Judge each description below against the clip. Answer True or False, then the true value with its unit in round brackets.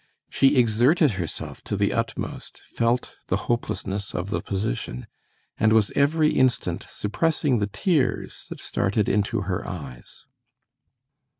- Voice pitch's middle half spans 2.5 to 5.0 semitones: False (5.4 semitones)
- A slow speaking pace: True (125 wpm)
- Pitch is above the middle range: False (110 Hz)